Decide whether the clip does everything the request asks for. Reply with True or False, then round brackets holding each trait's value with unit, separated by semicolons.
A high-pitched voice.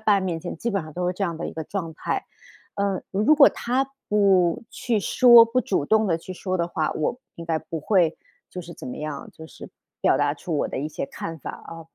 False (180 Hz)